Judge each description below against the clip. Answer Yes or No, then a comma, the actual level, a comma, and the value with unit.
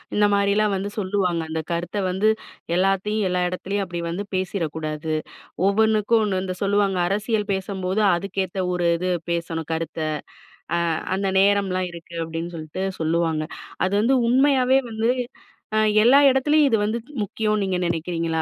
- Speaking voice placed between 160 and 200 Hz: Yes, high, 190 Hz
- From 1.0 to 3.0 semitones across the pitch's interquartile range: No, average, 3.5 semitones